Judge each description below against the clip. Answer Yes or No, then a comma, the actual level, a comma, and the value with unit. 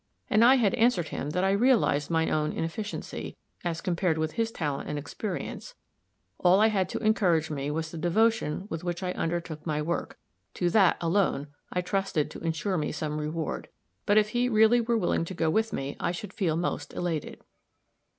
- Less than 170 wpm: No, average, 190 wpm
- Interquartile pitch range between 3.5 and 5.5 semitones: Yes, average, 5.0 semitones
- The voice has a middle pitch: Yes, medium, 175 Hz